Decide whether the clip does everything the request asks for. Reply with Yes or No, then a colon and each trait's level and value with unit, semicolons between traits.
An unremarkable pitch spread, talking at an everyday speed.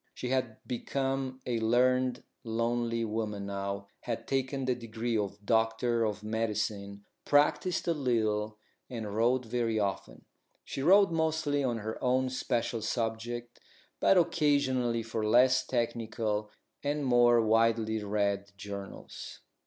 No: average, 3.0 semitones; slow, 125 wpm